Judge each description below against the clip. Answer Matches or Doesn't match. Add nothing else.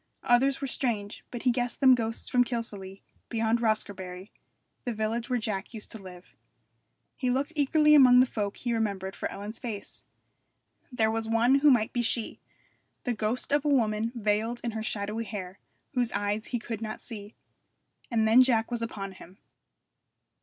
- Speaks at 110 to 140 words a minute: Doesn't match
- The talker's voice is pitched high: Matches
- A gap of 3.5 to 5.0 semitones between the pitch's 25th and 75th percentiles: Doesn't match